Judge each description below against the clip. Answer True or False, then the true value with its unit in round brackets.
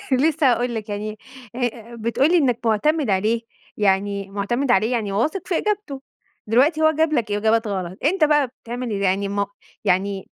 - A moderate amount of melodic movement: False (5.8 semitones)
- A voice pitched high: True (230 Hz)